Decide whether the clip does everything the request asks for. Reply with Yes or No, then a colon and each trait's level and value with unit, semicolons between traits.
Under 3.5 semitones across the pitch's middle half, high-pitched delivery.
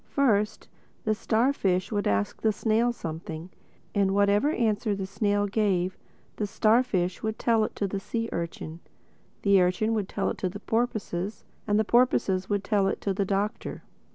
Yes: narrow, 2.4 semitones; high, 205 Hz